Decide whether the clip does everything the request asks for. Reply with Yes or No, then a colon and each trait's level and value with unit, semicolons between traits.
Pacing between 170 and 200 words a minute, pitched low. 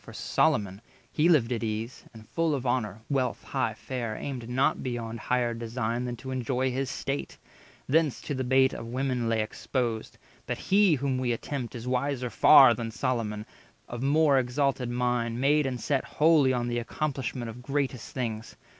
Yes: average, 180 wpm; low, 125 Hz